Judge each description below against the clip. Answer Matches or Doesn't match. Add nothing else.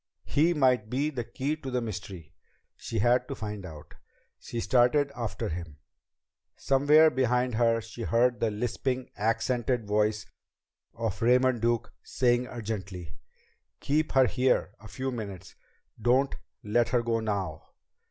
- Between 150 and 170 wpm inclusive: Doesn't match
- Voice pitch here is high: Doesn't match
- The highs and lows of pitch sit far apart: Doesn't match